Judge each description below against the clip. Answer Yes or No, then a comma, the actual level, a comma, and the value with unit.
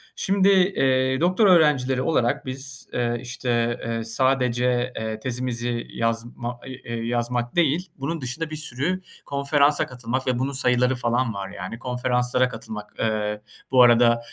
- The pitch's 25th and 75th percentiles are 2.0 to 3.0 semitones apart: Yes, narrow, 2.4 semitones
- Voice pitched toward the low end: Yes, low, 125 Hz